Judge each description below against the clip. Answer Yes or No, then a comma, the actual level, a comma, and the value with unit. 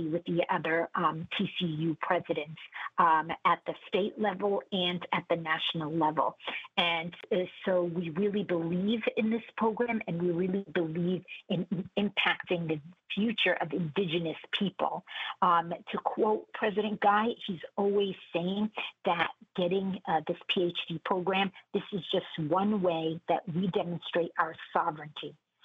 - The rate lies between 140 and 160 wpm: Yes, average, 145 wpm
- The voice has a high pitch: No, medium, 180 Hz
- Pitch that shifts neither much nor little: Yes, average, 3.1 semitones